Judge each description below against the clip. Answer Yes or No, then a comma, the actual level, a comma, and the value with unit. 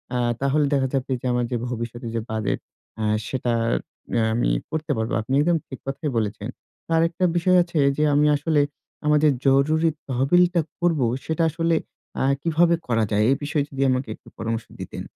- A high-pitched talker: No, medium, 140 Hz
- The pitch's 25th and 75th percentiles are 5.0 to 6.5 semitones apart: Yes, average, 5.3 semitones